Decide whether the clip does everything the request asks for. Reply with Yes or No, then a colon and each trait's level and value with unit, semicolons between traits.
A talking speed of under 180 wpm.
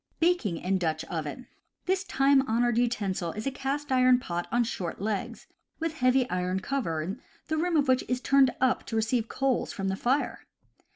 No: average, 185 wpm